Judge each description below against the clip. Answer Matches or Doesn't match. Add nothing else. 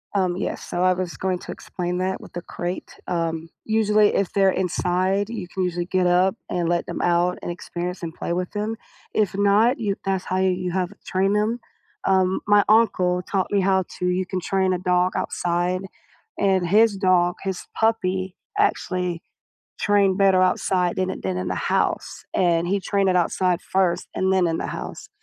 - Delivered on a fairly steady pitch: Matches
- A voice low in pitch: Doesn't match